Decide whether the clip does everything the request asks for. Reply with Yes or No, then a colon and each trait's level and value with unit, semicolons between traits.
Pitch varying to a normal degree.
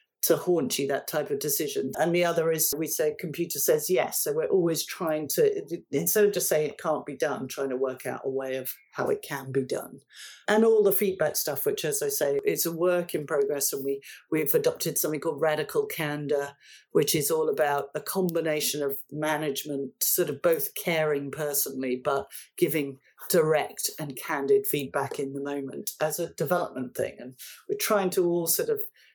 No: wide, 7.5 semitones